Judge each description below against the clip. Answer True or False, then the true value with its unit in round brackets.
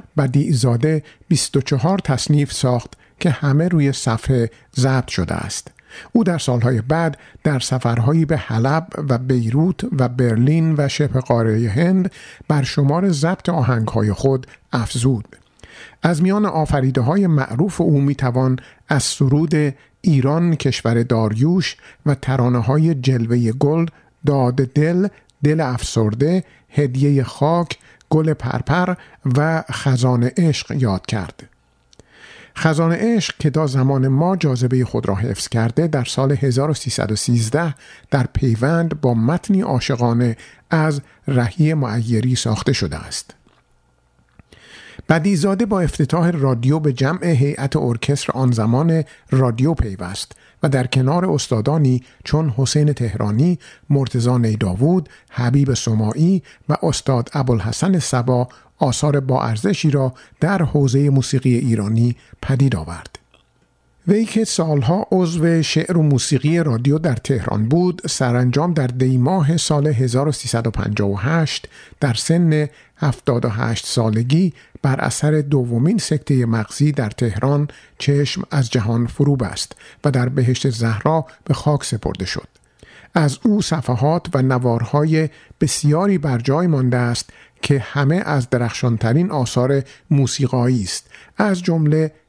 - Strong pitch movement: False (4.2 semitones)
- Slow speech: False (120 wpm)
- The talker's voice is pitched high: False (140 Hz)